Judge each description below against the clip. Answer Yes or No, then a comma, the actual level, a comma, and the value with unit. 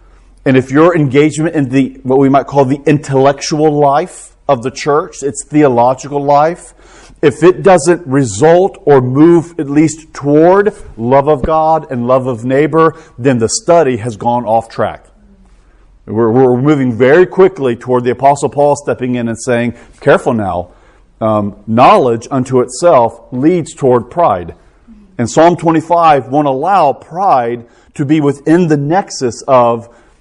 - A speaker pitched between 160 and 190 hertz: No, medium, 140 Hz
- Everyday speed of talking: Yes, average, 150 wpm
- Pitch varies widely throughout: No, average, 4.1 semitones